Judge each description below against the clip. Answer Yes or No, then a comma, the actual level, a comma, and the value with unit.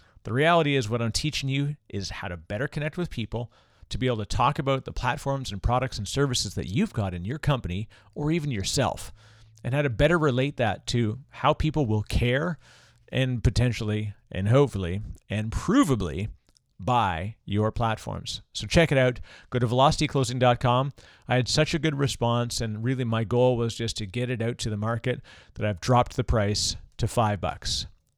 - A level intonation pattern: No, average, 4.2 semitones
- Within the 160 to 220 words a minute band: Yes, average, 190 wpm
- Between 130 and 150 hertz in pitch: No, low, 120 Hz